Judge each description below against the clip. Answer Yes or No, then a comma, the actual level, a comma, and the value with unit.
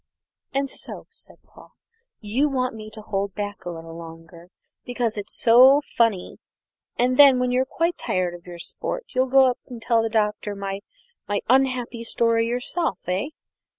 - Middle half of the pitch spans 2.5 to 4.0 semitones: No, average, 4.4 semitones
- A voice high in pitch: Yes, high, 230 Hz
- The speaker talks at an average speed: Yes, average, 170 wpm